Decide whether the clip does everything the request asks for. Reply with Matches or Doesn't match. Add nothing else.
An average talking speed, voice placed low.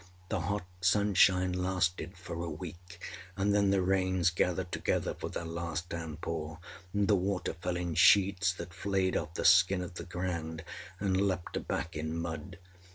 Matches